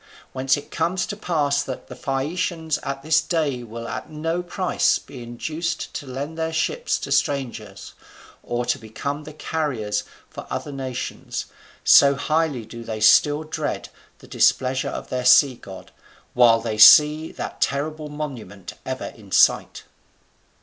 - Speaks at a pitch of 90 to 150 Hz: Yes, medium, 140 Hz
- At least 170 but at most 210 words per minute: No, average, 150 wpm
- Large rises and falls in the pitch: No, average, 4.3 semitones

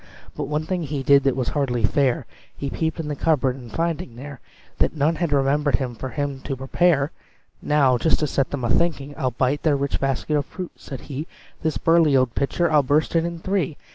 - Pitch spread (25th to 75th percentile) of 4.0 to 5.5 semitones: No, average, 2.9 semitones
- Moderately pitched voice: Yes, medium, 145 Hz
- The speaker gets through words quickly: Yes, fast, 215 wpm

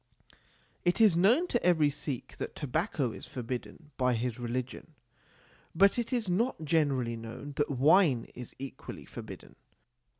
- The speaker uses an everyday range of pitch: No, wide, 6.1 semitones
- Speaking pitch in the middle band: Yes, medium, 145 Hz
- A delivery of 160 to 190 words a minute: No, average, 140 wpm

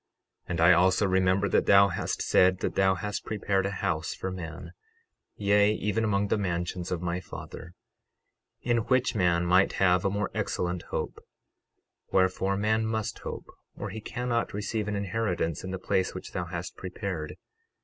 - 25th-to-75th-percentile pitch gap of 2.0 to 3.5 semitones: Yes, narrow, 2.5 semitones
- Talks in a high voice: No, very low, 95 Hz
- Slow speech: No, average, 170 wpm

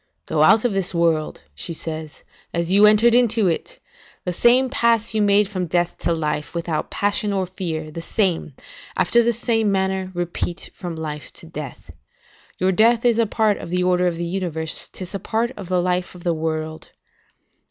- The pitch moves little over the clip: No, average, 4.1 semitones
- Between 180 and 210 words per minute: Yes, average, 190 wpm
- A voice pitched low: No, medium, 185 Hz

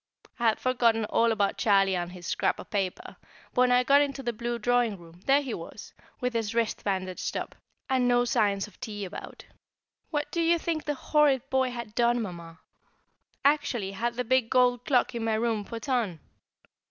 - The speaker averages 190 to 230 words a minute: Yes, average, 195 wpm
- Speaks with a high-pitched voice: Yes, high, 235 Hz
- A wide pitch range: No, average, 3.7 semitones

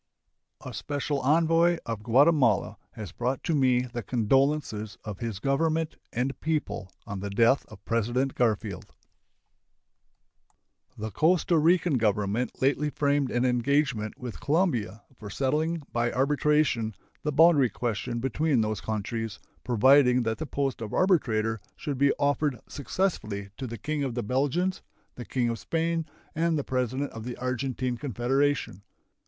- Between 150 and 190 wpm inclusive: No, average, 140 wpm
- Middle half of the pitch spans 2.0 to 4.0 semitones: No, average, 4.7 semitones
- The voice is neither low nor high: No, low, 130 Hz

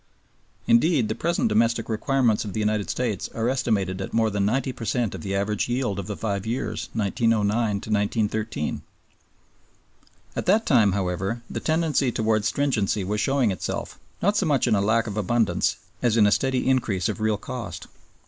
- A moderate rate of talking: Yes, average, 175 wpm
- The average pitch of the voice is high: No, low, 110 Hz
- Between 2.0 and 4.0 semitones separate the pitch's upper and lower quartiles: Yes, average, 3.3 semitones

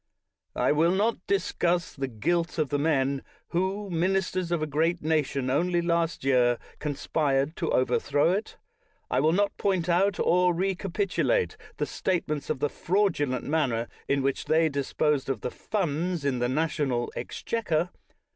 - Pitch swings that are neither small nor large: Yes, average, 4.4 semitones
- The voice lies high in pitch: No, medium, 160 Hz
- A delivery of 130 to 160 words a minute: Yes, average, 155 wpm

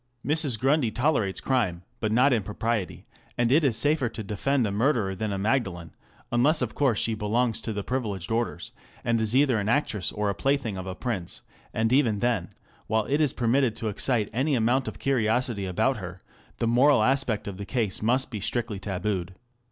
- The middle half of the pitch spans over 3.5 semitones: Yes, average, 4.0 semitones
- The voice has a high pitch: No, low, 115 Hz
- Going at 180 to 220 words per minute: Yes, average, 190 wpm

